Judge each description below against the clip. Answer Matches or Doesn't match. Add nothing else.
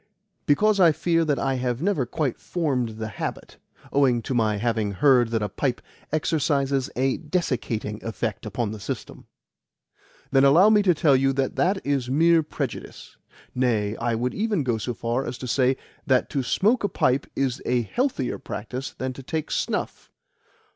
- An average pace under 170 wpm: Doesn't match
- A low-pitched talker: Matches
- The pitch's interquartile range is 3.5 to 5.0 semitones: Matches